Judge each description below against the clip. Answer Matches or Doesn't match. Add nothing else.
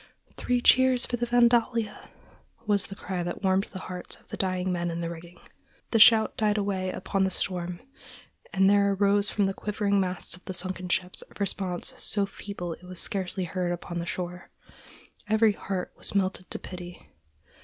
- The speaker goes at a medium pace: Matches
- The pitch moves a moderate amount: Doesn't match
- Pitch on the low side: Doesn't match